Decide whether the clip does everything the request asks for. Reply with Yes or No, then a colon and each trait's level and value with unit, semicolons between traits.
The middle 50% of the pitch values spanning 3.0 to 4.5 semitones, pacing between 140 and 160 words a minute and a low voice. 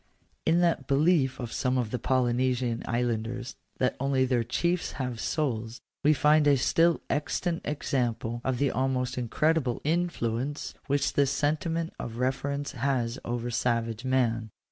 Yes: average, 3.4 semitones; average, 145 wpm; low, 130 Hz